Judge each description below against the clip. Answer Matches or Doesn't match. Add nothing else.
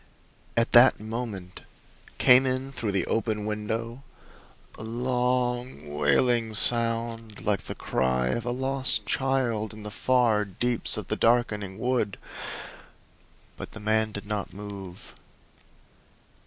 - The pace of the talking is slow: Matches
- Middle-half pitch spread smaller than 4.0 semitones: Matches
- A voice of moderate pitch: Doesn't match